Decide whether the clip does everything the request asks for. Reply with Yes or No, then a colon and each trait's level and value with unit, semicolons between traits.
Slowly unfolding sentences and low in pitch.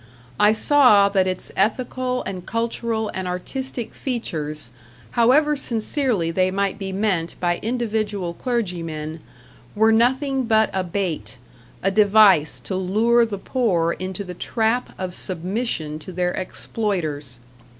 No: slow, 130 wpm; high, 200 Hz